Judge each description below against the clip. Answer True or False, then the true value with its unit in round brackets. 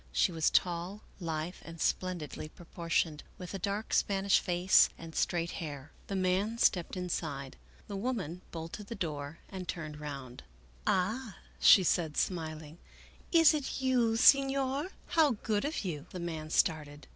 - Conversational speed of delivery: True (155 wpm)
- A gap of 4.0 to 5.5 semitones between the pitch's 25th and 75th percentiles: True (4.6 semitones)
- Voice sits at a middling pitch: True (175 Hz)